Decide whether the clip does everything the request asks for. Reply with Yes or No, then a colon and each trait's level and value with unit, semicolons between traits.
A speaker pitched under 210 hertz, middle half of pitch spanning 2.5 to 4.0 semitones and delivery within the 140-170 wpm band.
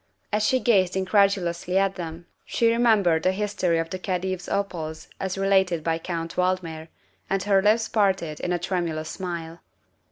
Yes: medium, 185 Hz; average, 2.8 semitones; average, 160 wpm